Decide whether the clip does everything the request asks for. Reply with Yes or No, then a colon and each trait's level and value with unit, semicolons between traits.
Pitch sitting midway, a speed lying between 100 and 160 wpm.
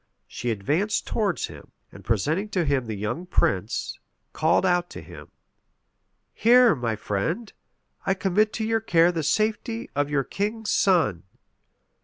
Yes: medium, 175 Hz; average, 145 wpm